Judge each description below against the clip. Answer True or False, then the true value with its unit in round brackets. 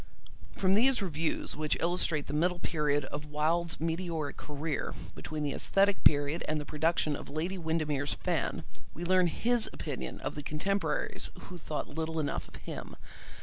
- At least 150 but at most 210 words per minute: True (160 wpm)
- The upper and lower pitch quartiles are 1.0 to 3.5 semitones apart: True (2.9 semitones)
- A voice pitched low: False (160 Hz)